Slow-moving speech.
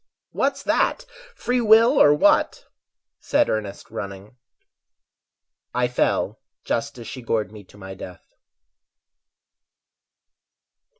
Yes: slow, 105 wpm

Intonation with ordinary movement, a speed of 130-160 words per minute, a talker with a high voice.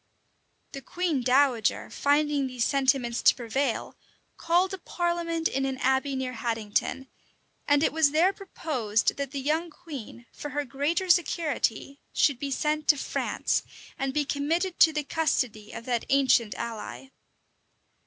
Yes: average, 3.9 semitones; average, 150 wpm; very high, 280 Hz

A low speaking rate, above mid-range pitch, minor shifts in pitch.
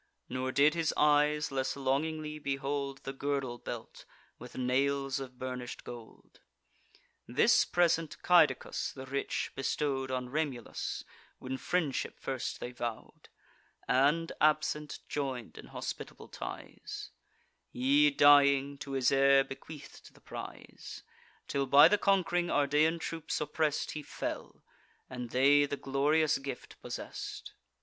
No: slow, 125 wpm; medium, 140 Hz; narrow, 2.3 semitones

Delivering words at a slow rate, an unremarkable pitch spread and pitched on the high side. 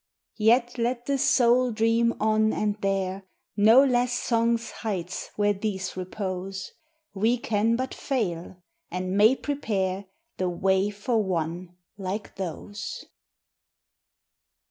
Yes: slow, 120 wpm; average, 3.7 semitones; high, 210 Hz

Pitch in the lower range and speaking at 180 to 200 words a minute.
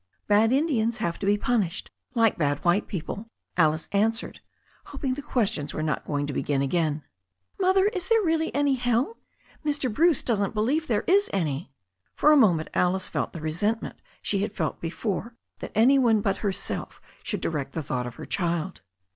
No: high, 210 Hz; average, 185 wpm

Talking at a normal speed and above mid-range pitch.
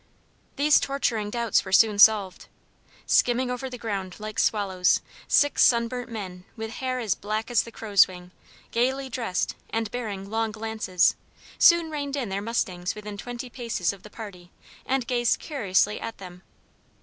Yes: average, 160 wpm; high, 220 Hz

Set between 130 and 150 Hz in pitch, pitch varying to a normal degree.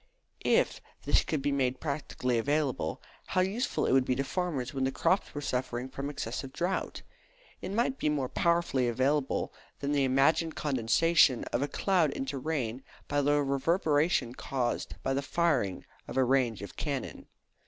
Yes: medium, 140 Hz; average, 3.3 semitones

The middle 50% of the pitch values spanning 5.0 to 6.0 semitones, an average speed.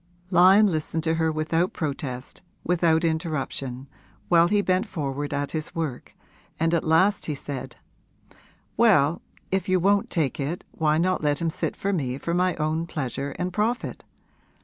No: average, 3.6 semitones; average, 160 wpm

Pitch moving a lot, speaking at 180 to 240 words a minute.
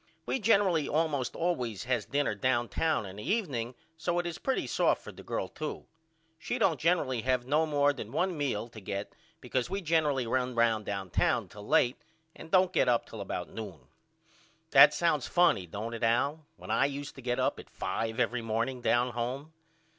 Yes: wide, 5.7 semitones; average, 190 wpm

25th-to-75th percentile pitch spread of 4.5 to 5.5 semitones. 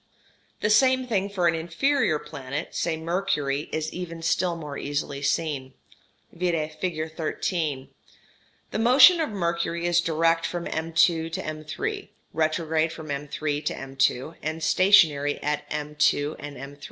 No: narrow, 2.6 semitones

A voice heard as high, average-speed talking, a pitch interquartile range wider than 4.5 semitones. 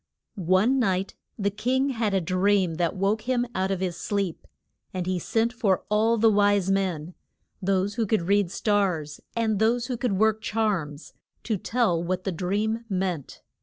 No: high, 200 Hz; average, 170 wpm; average, 3.1 semitones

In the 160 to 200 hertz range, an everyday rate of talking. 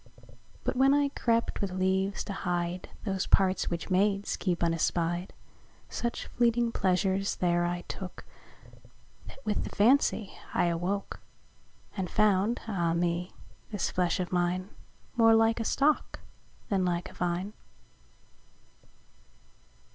No: high, 190 Hz; slow, 125 wpm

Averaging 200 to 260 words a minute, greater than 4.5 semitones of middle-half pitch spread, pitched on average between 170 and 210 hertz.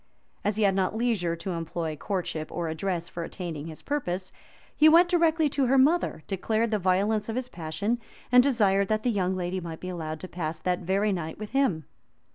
Yes: fast, 205 wpm; average, 5.3 semitones; high, 190 Hz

